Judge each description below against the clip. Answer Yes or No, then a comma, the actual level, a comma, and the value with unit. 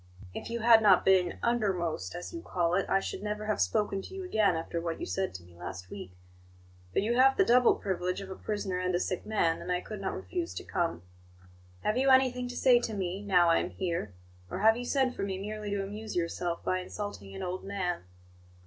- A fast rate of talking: Yes, fast, 230 wpm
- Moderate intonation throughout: Yes, average, 3.9 semitones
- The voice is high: Yes, high, 195 Hz